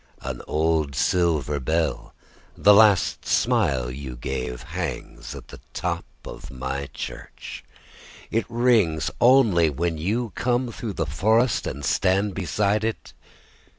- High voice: No, very low, 85 Hz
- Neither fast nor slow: No, slow, 115 wpm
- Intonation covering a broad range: Yes, wide, 7.4 semitones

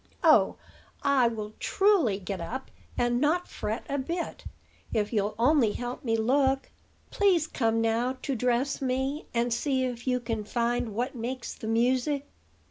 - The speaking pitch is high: Yes, high, 245 Hz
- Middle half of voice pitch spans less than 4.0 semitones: Yes, average, 3.3 semitones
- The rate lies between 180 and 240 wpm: No, average, 155 wpm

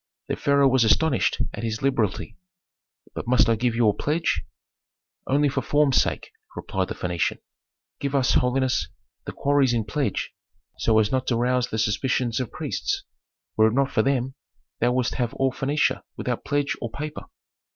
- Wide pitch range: No, average, 3.2 semitones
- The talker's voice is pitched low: Yes, low, 125 Hz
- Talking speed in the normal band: Yes, average, 170 wpm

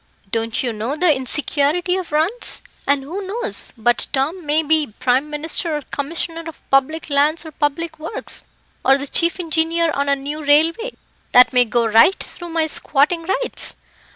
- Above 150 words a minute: Yes, average, 170 wpm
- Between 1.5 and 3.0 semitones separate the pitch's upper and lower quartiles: No, average, 3.4 semitones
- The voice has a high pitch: Yes, very high, 305 Hz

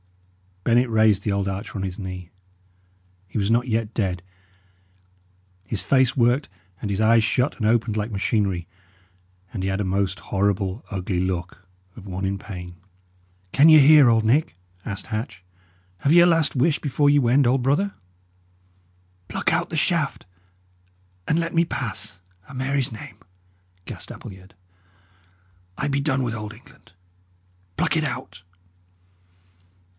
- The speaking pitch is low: Yes, low, 110 Hz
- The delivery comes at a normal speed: Yes, average, 150 wpm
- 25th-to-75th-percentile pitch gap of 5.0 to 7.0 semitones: Yes, wide, 5.6 semitones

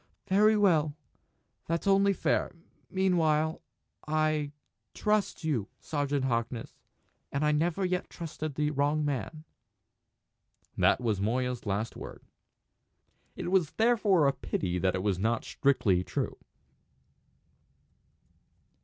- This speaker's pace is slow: Yes, slow, 110 wpm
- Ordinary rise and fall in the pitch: No, wide, 6.4 semitones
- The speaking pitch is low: No, medium, 150 Hz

